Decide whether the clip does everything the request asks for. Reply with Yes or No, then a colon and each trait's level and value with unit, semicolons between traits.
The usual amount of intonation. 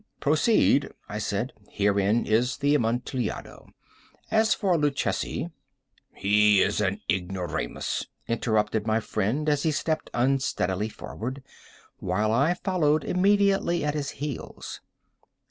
No: wide, 6.3 semitones